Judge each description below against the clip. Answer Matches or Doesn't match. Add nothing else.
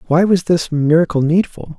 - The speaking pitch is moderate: Matches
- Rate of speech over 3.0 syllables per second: Matches